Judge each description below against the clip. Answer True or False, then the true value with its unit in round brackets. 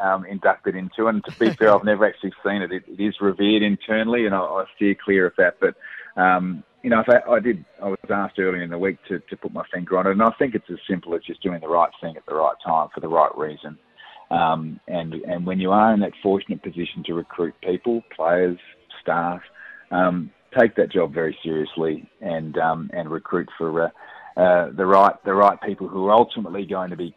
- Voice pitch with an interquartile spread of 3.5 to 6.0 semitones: False (2.5 semitones)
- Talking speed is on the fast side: True (230 wpm)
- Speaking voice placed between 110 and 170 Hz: False (95 Hz)